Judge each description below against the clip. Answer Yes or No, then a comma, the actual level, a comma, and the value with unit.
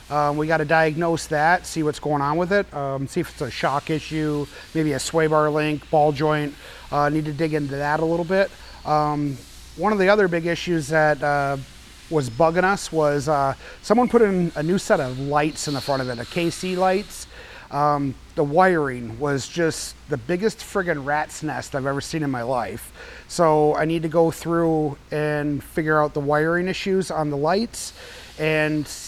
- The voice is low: No, medium, 155 Hz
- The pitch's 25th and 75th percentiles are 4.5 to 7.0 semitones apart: No, average, 2.7 semitones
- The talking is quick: Yes, fast, 210 wpm